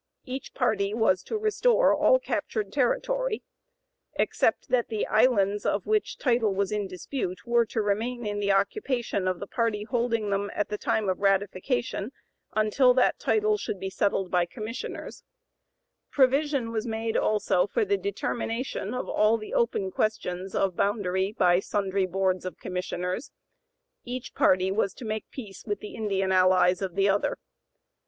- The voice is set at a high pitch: Yes, high, 210 Hz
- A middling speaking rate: Yes, average, 160 wpm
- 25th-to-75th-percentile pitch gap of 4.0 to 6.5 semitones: Yes, average, 4.3 semitones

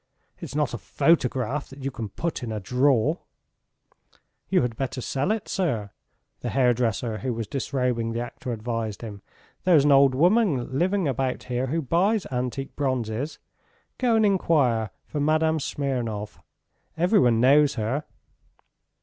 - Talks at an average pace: Yes, average, 145 wpm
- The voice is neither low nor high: No, low, 130 Hz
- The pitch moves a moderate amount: Yes, average, 4.7 semitones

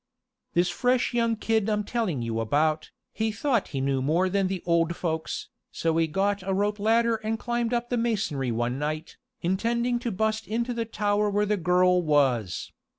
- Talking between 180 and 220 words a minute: Yes, average, 185 wpm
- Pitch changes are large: Yes, wide, 5.9 semitones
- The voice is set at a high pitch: Yes, high, 200 Hz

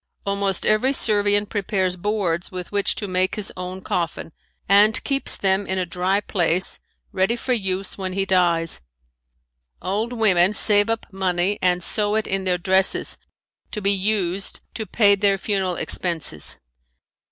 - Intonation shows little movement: Yes, narrow, 2.2 semitones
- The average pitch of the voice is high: Yes, high, 195 Hz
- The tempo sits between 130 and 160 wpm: Yes, average, 150 wpm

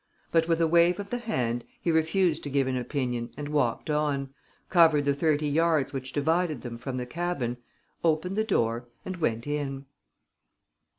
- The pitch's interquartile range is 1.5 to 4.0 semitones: No, average, 4.4 semitones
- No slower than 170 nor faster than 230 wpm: Yes, average, 175 wpm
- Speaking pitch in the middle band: Yes, medium, 150 Hz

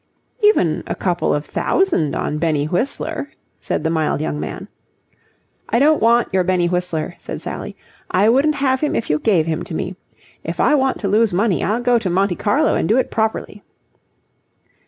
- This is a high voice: Yes, high, 200 Hz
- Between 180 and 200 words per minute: Yes, average, 185 wpm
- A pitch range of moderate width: No, wide, 6.9 semitones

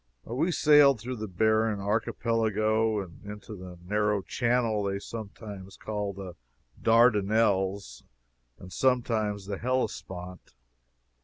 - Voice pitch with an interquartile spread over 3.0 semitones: No, average, 2.7 semitones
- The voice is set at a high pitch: No, low, 105 Hz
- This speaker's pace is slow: Yes, slow, 105 wpm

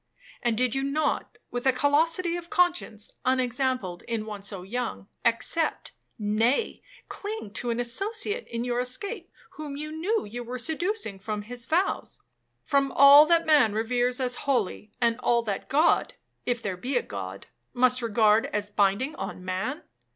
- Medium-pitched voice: No, very high, 250 Hz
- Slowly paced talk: No, average, 160 wpm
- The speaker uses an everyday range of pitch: No, wide, 5.7 semitones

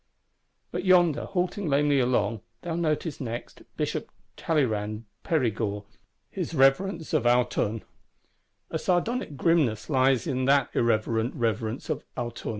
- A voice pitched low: Yes, low, 130 Hz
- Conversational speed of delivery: No, slow, 120 wpm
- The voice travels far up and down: Yes, wide, 5.9 semitones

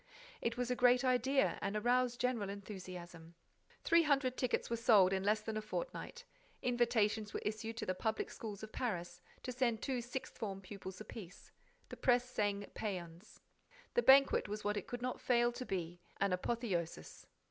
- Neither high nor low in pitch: No, high, 220 Hz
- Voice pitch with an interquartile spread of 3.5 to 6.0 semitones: Yes, average, 4.0 semitones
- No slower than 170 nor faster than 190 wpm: Yes, average, 175 wpm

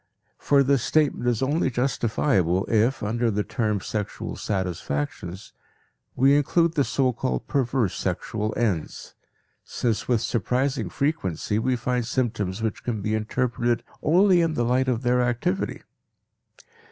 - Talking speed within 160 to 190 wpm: No, slow, 135 wpm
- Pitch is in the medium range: No, low, 120 Hz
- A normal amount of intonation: Yes, average, 4.1 semitones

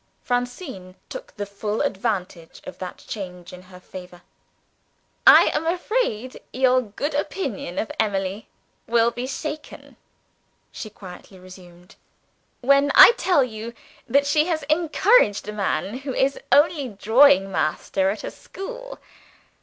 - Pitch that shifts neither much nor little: No, wide, 7.0 semitones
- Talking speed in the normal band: No, slow, 130 wpm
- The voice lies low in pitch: No, high, 230 Hz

